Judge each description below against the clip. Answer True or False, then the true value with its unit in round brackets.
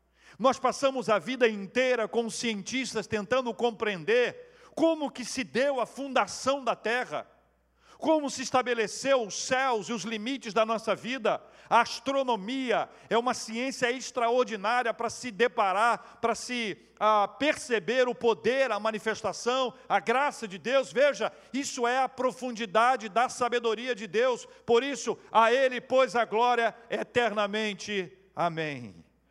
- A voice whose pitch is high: True (235 Hz)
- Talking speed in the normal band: True (140 wpm)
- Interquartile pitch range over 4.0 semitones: False (2.9 semitones)